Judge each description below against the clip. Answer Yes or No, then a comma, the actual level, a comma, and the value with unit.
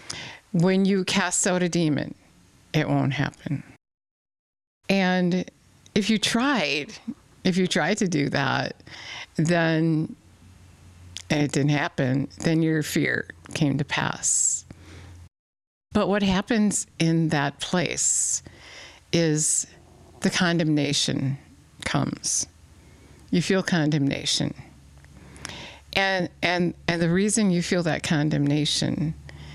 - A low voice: No, medium, 155 Hz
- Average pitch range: No, wide, 5.9 semitones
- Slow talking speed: Yes, slow, 105 wpm